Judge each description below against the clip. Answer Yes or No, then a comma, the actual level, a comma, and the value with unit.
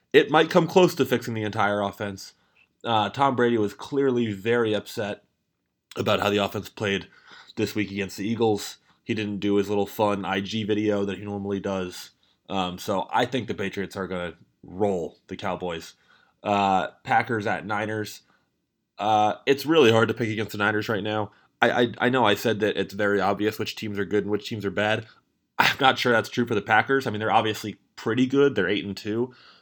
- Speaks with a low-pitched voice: Yes, low, 105 Hz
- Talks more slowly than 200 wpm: No, fast, 205 wpm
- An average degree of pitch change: No, narrow, 2.1 semitones